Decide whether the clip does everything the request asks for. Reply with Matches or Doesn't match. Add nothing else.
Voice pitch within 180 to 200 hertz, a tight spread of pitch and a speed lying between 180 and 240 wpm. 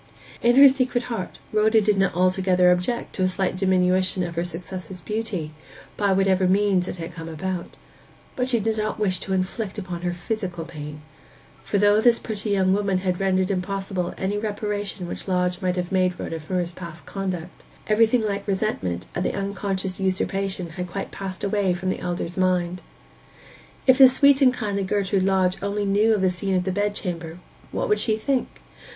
Matches